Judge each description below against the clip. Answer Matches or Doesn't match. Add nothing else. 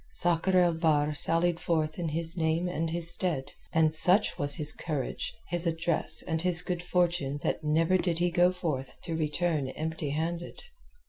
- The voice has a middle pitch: Matches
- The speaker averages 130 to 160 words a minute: Doesn't match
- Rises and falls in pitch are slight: Matches